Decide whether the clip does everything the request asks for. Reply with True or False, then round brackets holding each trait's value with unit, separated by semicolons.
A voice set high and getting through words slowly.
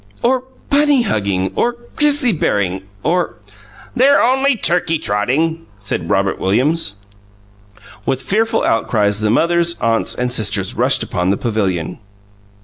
False (140 Hz; 130 wpm)